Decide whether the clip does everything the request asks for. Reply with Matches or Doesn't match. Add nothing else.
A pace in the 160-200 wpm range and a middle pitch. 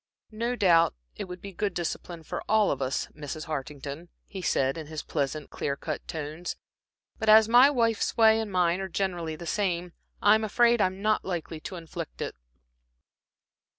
Matches